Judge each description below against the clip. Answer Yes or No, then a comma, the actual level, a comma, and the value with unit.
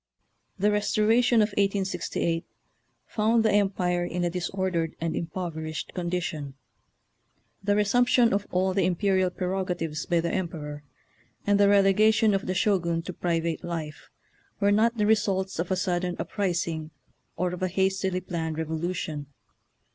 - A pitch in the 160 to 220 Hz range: Yes, medium, 185 Hz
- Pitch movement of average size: Yes, average, 3.1 semitones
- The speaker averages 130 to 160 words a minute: Yes, average, 145 wpm